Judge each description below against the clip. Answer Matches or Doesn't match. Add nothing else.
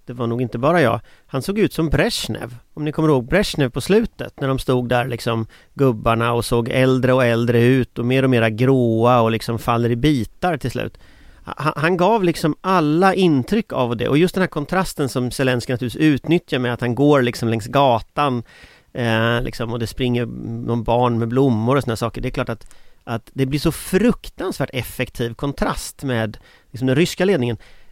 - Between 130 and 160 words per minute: Doesn't match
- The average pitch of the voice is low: Matches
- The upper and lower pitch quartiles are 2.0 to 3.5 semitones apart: Doesn't match